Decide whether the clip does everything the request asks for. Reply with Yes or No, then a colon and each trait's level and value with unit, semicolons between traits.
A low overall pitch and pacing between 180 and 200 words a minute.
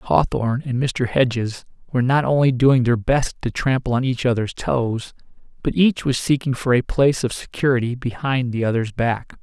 Yes: low, 125 Hz; average, 185 wpm